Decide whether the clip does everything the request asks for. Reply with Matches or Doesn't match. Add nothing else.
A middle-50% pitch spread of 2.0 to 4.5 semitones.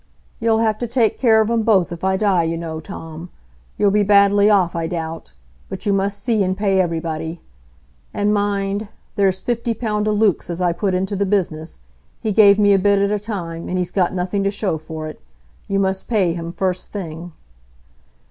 Matches